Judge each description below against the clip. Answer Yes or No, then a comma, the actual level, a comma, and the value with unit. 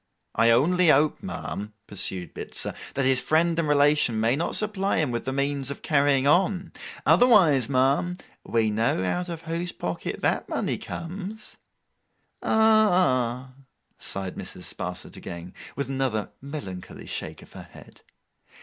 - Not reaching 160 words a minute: Yes, average, 140 wpm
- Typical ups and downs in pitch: No, wide, 6.7 semitones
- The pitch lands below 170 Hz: Yes, medium, 140 Hz